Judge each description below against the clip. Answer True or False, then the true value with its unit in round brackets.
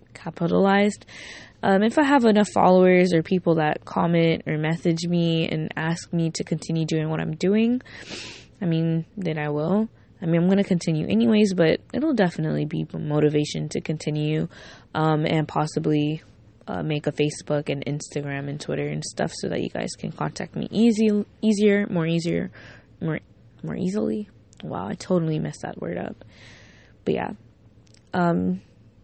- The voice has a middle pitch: True (160 Hz)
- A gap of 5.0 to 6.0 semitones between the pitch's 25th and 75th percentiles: False (4.0 semitones)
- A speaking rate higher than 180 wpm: False (165 wpm)